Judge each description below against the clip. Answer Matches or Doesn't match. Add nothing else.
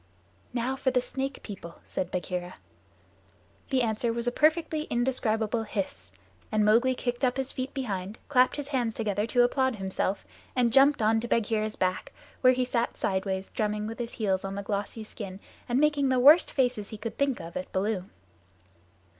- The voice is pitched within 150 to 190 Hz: Doesn't match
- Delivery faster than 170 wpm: Matches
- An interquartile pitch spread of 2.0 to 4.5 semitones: Matches